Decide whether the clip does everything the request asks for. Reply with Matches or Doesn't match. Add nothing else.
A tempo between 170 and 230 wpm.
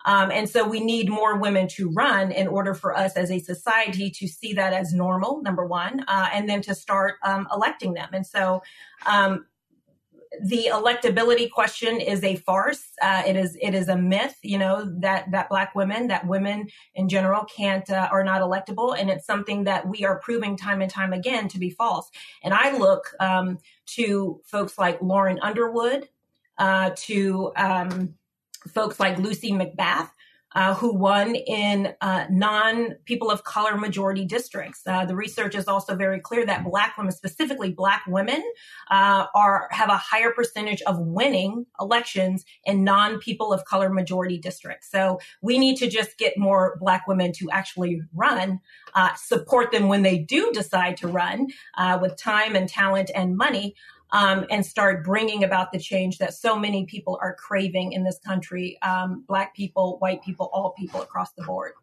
Matches